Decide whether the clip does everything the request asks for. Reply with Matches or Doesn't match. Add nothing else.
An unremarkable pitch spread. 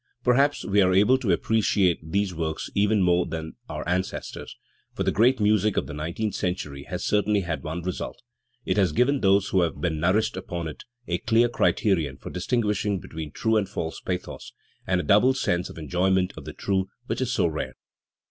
Matches